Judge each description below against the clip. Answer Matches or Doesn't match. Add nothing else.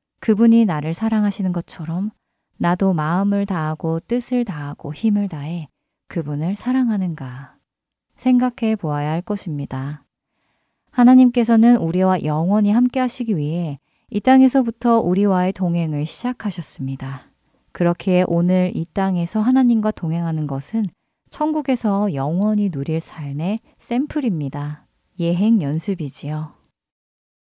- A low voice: Doesn't match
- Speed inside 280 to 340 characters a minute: Matches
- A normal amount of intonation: Doesn't match